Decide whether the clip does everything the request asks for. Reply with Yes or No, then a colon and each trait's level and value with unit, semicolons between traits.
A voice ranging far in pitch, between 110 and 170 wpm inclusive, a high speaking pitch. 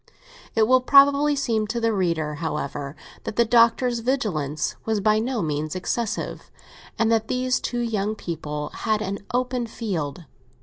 Yes: wide, 6.3 semitones; average, 150 wpm; high, 220 Hz